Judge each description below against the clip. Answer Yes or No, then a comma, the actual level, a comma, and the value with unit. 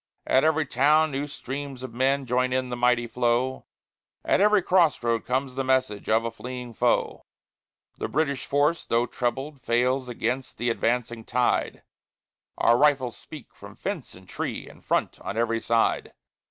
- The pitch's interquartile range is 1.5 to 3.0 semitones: Yes, narrow, 2.6 semitones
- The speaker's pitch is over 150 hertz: No, low, 125 Hz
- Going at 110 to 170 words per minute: Yes, average, 160 wpm